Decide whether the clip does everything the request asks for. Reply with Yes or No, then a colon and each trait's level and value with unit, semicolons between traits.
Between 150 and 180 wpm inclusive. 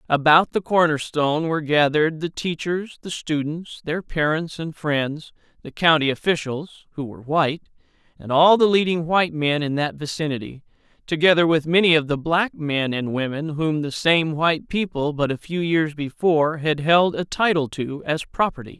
Yes: average, 170 wpm